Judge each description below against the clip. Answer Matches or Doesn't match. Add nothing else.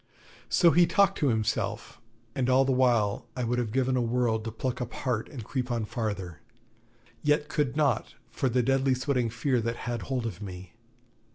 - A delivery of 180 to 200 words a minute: Matches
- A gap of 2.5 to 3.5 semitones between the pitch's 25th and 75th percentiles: Matches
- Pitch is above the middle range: Doesn't match